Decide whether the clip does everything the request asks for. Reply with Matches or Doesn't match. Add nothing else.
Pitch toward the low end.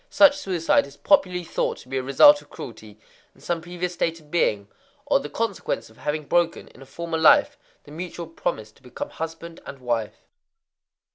Doesn't match